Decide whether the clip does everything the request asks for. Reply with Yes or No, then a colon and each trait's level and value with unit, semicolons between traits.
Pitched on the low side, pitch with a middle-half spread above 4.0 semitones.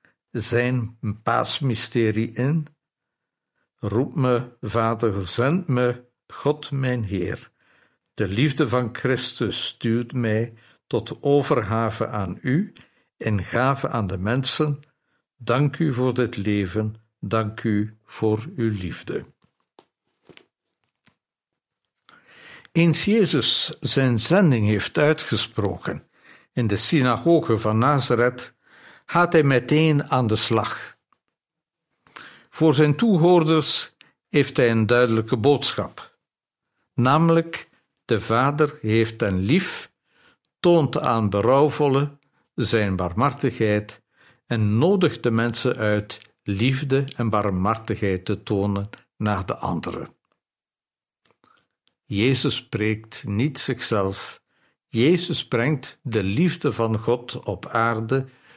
Yes: low, 120 Hz; average, 4.7 semitones